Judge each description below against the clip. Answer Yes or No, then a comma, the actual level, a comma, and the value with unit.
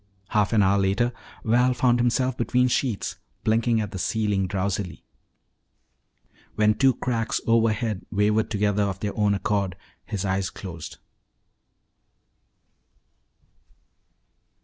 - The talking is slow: Yes, slow, 110 wpm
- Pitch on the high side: No, low, 105 Hz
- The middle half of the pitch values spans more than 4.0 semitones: No, average, 2.9 semitones